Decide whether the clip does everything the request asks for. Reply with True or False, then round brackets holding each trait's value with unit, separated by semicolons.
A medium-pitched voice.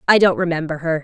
True (165 Hz)